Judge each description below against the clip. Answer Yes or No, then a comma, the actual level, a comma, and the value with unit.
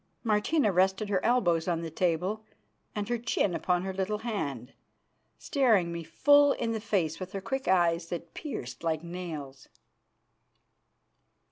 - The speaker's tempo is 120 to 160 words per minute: Yes, average, 145 wpm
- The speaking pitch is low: No, medium, 185 Hz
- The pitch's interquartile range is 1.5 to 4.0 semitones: No, average, 4.5 semitones